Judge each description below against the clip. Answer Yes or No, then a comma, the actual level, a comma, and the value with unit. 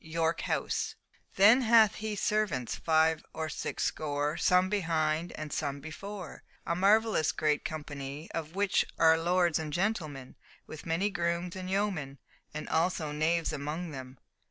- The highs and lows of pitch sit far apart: No, average, 3.6 semitones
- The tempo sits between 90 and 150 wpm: Yes, average, 145 wpm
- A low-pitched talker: No, medium, 165 Hz